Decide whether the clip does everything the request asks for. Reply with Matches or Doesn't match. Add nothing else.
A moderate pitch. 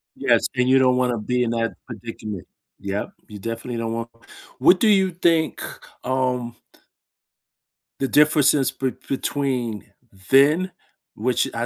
Doesn't match